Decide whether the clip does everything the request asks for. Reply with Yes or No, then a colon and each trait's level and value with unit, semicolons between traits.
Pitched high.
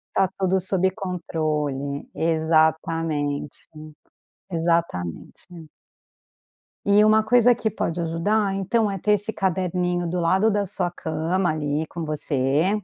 No: medium, 175 Hz